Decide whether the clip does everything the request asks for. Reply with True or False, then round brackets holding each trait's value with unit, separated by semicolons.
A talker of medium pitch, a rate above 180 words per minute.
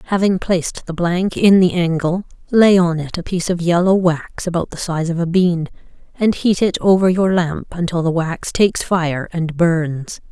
True (175 Hz; 200 wpm)